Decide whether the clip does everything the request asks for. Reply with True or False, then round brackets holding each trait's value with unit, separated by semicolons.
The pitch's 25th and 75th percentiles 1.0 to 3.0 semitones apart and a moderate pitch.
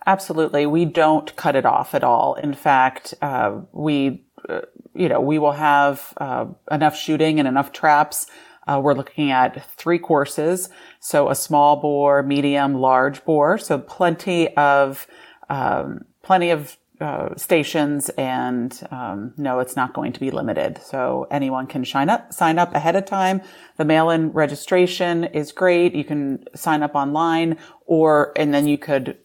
True (2.7 semitones; 150 Hz)